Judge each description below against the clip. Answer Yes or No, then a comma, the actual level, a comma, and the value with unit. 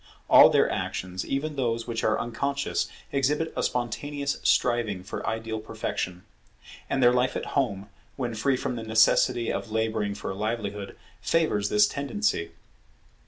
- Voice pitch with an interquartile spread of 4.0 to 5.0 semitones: Yes, average, 4.5 semitones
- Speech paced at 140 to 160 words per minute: Yes, average, 150 wpm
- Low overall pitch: Yes, low, 115 Hz